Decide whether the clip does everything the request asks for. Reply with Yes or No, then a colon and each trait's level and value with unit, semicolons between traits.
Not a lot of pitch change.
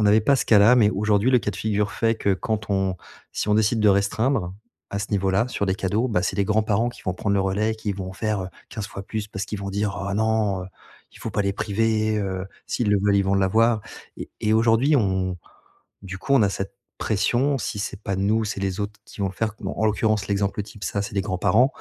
Yes: narrow, 2.0 semitones